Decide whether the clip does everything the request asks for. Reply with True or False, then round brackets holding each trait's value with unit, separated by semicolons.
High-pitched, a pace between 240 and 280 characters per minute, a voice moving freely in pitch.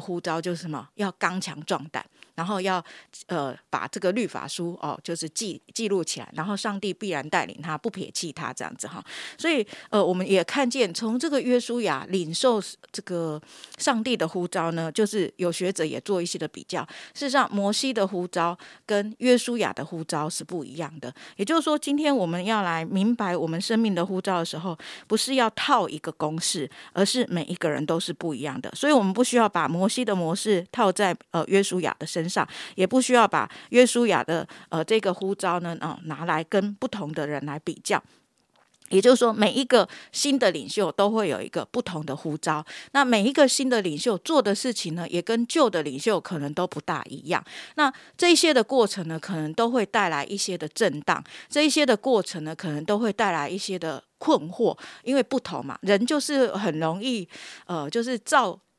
False (195 Hz; 300 characters per minute; 5.9 semitones)